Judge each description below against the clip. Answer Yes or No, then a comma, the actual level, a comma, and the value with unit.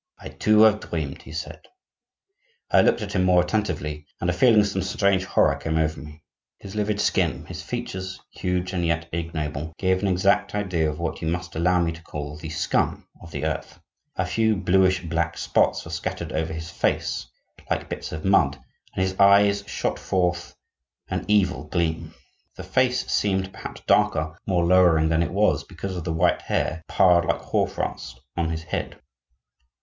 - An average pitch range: Yes, average, 3.0 semitones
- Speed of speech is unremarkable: Yes, average, 185 wpm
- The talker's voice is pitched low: Yes, very low, 90 Hz